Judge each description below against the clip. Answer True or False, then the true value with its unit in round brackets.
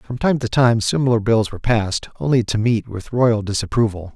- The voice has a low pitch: True (115 Hz)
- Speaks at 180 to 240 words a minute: True (200 wpm)